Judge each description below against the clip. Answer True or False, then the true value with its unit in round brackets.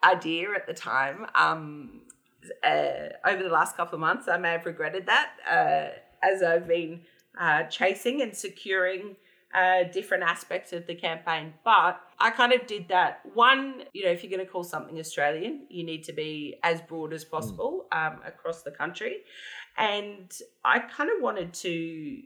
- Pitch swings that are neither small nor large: False (6.6 semitones)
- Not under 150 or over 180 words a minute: True (175 wpm)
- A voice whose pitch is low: False (185 Hz)